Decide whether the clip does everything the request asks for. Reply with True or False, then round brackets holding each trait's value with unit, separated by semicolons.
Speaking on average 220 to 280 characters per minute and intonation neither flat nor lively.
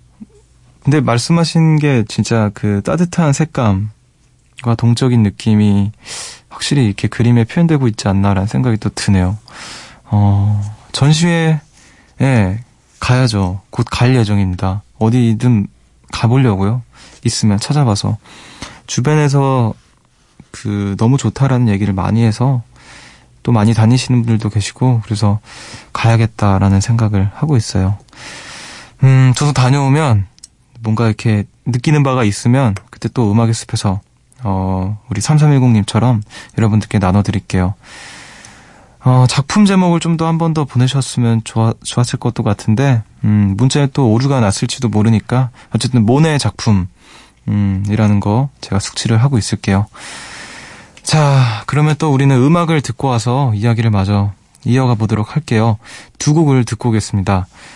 False (295 characters per minute; 4.0 semitones)